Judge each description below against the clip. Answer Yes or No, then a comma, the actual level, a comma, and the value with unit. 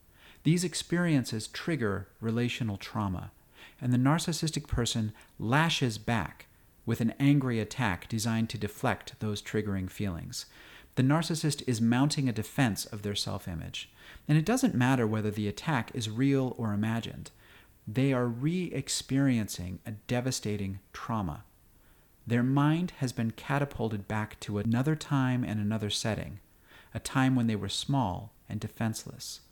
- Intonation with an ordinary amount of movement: Yes, average, 4.2 semitones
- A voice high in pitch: No, low, 115 Hz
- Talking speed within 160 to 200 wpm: No, average, 140 wpm